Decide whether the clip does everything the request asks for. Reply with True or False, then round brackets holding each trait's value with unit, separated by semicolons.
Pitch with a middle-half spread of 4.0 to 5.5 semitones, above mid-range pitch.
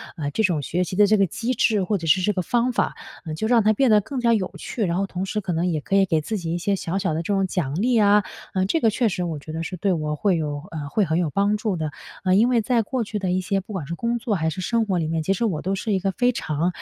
True (4.3 semitones; 195 Hz)